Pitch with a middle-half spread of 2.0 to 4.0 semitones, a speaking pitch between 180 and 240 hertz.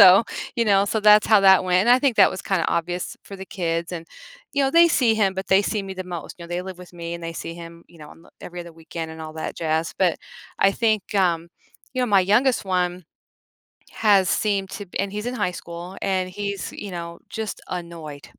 Yes: average, 3.2 semitones; medium, 185 Hz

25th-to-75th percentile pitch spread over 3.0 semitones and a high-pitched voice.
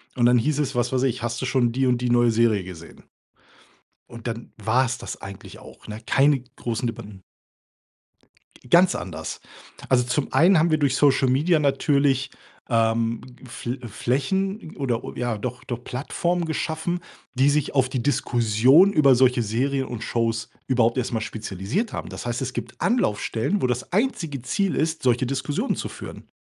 No: average, 3.7 semitones; low, 130 Hz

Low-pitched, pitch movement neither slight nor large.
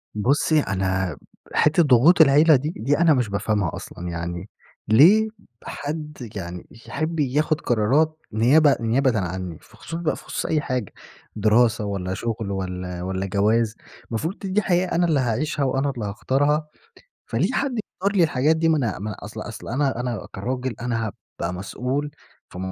No: low, 125 Hz; wide, 6.9 semitones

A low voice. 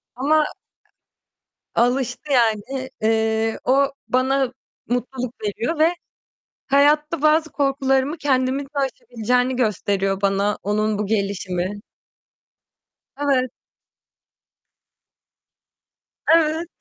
No: very high, 255 Hz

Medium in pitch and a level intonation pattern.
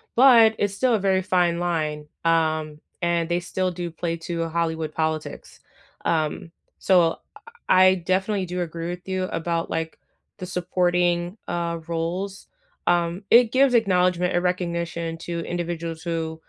Yes: medium, 175 Hz; narrow, 1.9 semitones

